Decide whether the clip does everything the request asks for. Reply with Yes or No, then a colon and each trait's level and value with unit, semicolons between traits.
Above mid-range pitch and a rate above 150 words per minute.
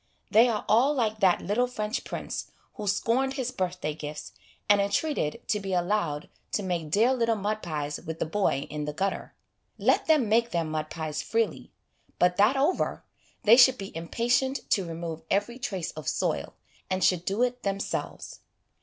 Yes: high, 200 Hz; average, 175 wpm